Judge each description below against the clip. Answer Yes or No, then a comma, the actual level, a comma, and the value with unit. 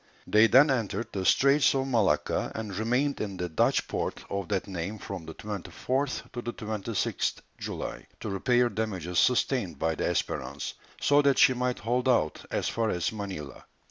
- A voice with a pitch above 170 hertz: No, low, 110 Hz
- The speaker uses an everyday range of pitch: Yes, average, 4.9 semitones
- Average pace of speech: Yes, average, 175 wpm